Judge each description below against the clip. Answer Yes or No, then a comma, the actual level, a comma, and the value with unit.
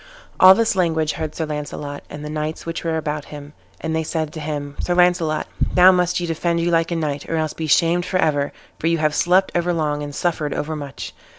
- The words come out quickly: Yes, fast, 220 wpm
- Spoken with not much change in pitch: Yes, narrow, 2.3 semitones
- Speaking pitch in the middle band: Yes, medium, 160 Hz